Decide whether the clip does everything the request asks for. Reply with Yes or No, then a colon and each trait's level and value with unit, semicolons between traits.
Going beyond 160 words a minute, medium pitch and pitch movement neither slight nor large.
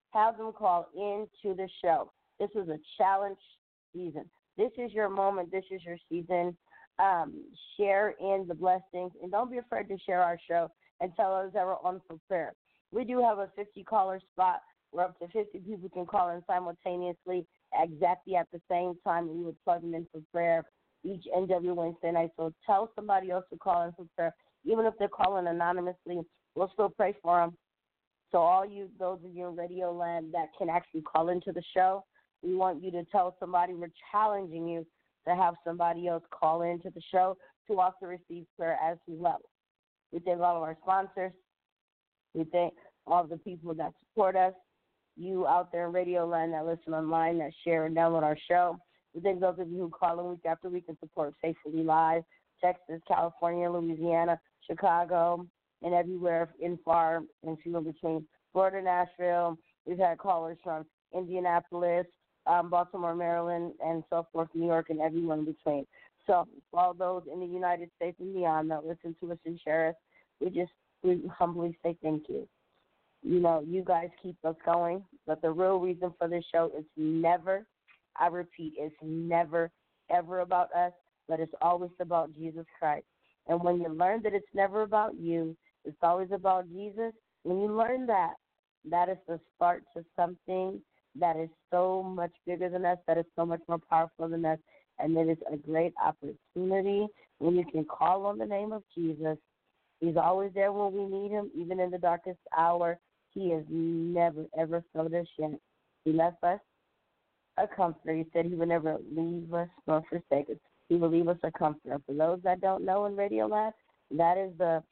No: average, 190 wpm; medium, 175 Hz; narrow, 2.0 semitones